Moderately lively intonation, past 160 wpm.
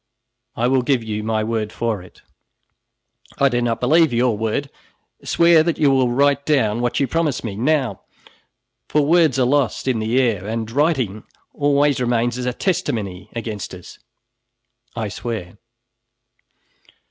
No: average, 4.3 semitones; average, 150 wpm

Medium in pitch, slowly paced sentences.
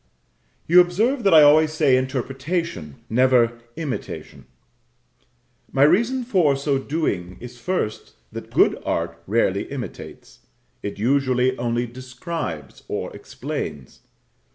No: low, 130 Hz; slow, 110 wpm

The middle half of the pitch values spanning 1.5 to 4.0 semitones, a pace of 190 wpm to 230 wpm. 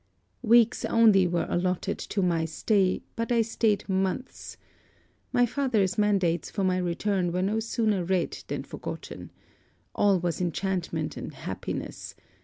No: average, 3.5 semitones; slow, 135 wpm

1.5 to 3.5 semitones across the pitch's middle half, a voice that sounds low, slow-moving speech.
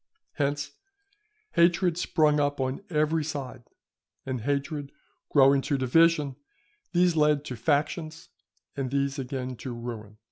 No: average, 2.9 semitones; medium, 145 Hz; slow, 120 wpm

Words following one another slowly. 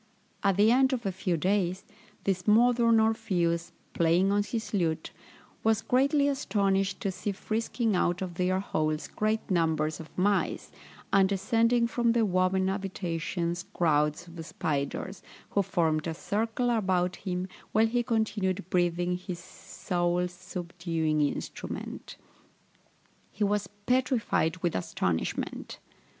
Yes: slow, 130 wpm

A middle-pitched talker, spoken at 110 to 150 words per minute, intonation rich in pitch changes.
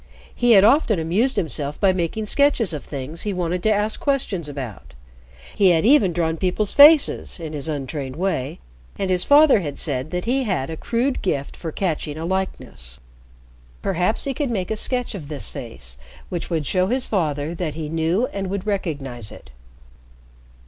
No: medium, 180 Hz; average, 180 wpm; wide, 5.9 semitones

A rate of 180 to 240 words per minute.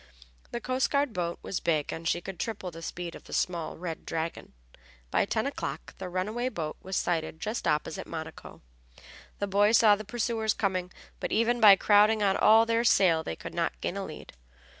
Yes: average, 195 wpm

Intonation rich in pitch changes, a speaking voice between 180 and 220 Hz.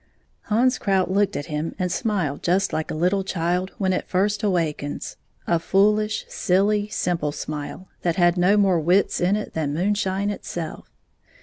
No: average, 3.2 semitones; medium, 185 Hz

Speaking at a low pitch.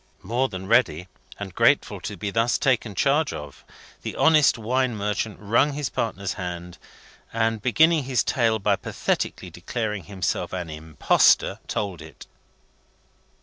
Yes: low, 110 Hz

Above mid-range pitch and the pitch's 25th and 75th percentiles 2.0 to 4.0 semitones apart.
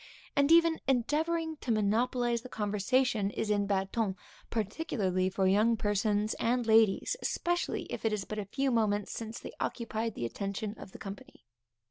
Yes: high, 220 Hz; average, 3.7 semitones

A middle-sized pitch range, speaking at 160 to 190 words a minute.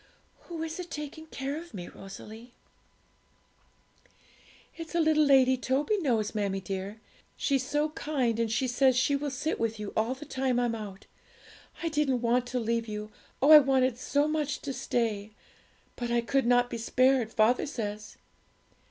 Yes: average, 4.2 semitones; average, 170 wpm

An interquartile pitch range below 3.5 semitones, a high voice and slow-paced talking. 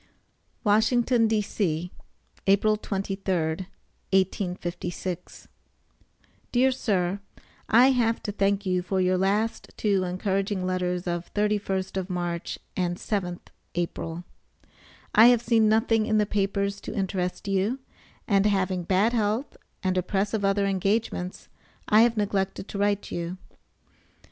Yes: narrow, 2.6 semitones; high, 195 Hz; slow, 125 wpm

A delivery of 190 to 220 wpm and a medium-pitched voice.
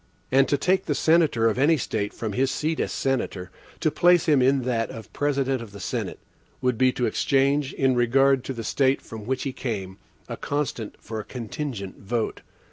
No: average, 200 wpm; low, 130 Hz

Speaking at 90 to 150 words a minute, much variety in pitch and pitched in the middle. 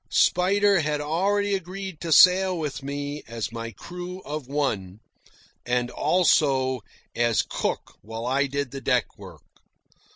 Yes: slow, 135 wpm; wide, 6.4 semitones; medium, 145 Hz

